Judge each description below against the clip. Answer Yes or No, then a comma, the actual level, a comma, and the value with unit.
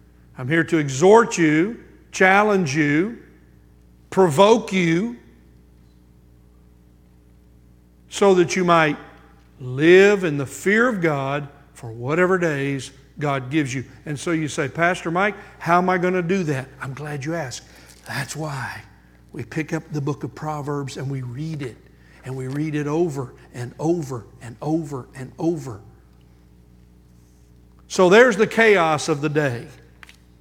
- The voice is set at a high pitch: No, medium, 140 Hz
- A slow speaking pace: No, average, 145 wpm